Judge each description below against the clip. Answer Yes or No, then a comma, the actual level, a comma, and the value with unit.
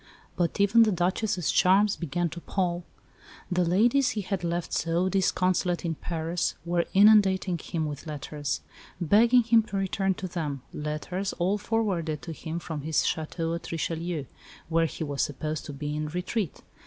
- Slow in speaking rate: No, average, 165 wpm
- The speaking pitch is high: No, medium, 175 Hz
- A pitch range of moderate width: Yes, average, 3.4 semitones